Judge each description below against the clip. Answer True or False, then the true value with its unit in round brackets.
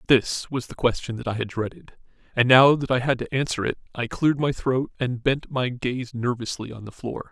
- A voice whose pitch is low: True (125 Hz)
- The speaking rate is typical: False (230 wpm)